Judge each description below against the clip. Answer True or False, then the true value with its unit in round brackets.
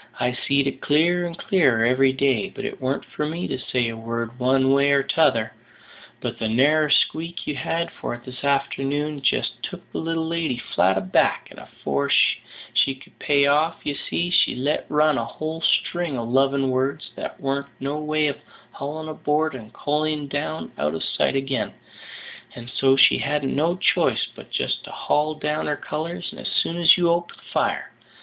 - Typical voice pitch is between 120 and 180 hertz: True (140 Hz)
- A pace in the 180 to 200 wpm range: True (190 wpm)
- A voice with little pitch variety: False (3.0 semitones)